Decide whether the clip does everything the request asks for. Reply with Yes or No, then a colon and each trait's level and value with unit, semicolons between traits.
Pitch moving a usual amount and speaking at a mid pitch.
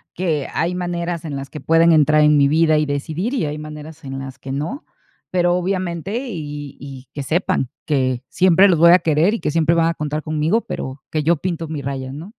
Yes: average, 3.0 semitones; medium, 155 Hz